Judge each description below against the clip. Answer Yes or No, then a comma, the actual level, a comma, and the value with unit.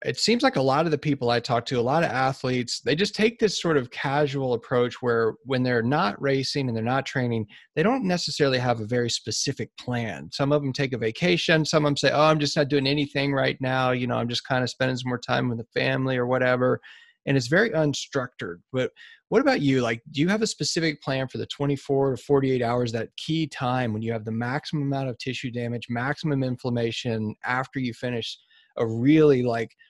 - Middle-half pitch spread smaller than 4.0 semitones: Yes, average, 3.5 semitones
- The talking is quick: Yes, fast, 230 wpm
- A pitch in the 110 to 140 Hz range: Yes, low, 130 Hz